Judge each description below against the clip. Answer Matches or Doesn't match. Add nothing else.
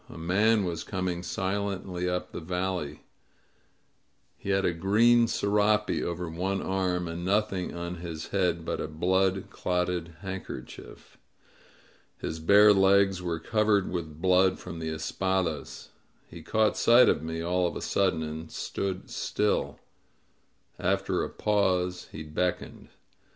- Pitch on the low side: Matches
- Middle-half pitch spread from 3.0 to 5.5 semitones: Doesn't match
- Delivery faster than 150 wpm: Doesn't match